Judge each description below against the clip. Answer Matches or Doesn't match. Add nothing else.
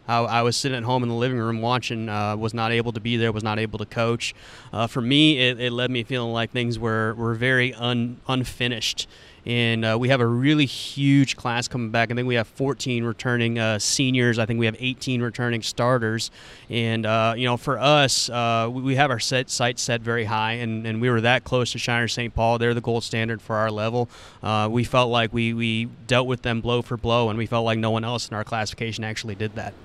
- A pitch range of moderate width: Doesn't match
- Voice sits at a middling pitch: Doesn't match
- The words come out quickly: Matches